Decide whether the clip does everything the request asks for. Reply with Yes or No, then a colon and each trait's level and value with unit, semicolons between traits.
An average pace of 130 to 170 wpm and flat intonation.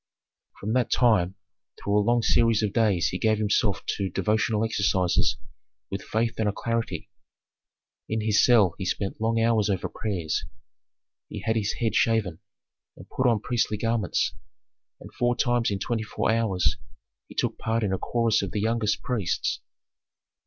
Yes: average, 160 wpm; narrow, 2.2 semitones